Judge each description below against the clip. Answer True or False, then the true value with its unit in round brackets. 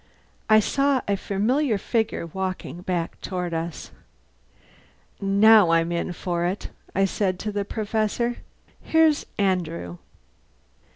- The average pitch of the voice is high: True (195 Hz)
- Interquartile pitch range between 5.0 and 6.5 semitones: False (3.7 semitones)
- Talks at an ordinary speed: False (115 wpm)